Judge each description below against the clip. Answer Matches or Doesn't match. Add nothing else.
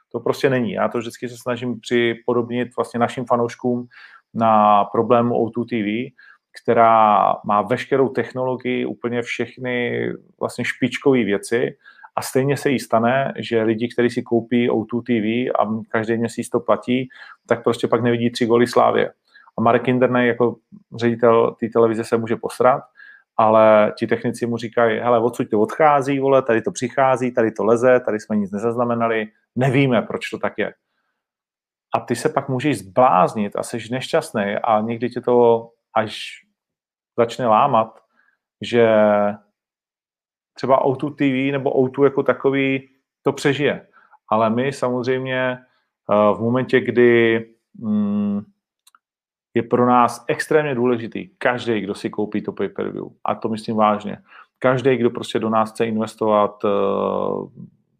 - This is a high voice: Doesn't match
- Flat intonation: Matches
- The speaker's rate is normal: Matches